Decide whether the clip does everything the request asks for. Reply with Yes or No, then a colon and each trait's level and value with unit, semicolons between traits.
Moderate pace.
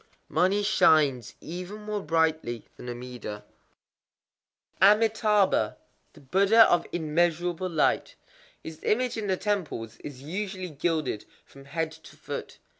No: slow, 120 wpm